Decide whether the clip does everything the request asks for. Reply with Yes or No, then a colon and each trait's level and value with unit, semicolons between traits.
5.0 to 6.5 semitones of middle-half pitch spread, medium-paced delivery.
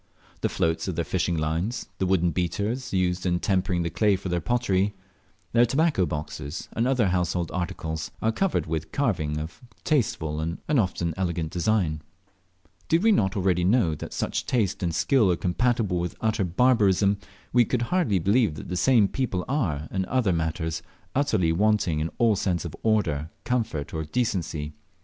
Yes: wide, 5.4 semitones; average, 170 wpm